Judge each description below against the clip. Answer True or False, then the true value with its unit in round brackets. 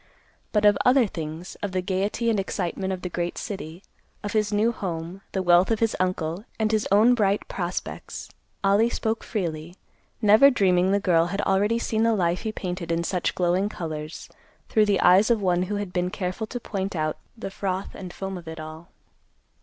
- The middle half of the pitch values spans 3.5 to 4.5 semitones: False (3.1 semitones)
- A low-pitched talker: False (190 Hz)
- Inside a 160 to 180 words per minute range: False (195 wpm)